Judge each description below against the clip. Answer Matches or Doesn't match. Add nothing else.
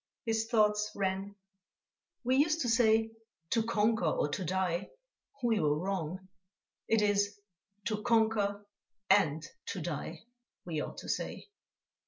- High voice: Matches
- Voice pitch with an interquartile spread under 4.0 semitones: Matches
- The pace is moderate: Doesn't match